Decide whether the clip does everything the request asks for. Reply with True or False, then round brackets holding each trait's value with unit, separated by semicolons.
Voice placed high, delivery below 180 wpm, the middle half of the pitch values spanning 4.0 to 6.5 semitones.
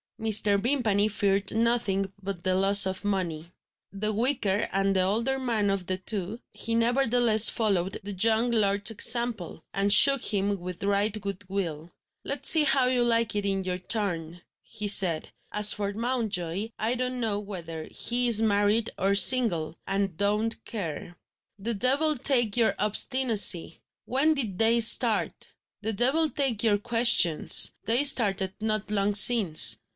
False (210 Hz; 155 wpm; 3.2 semitones)